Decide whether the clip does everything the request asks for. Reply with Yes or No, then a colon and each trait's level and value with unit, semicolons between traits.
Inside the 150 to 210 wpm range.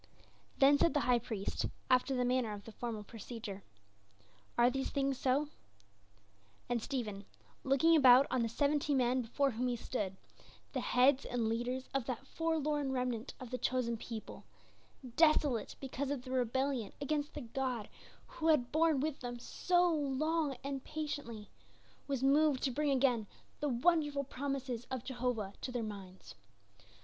Yes: average, 155 wpm